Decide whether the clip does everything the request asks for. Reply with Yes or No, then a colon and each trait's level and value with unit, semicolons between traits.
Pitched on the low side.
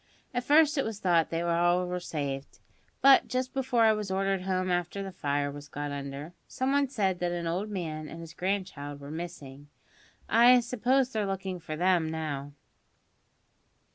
No: medium, 180 Hz